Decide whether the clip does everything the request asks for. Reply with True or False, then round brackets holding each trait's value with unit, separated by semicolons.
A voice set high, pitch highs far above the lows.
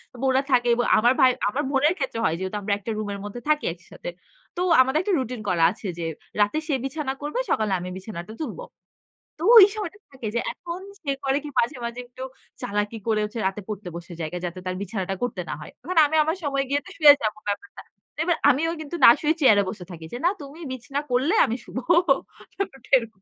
True (250 Hz; 6.1 semitones)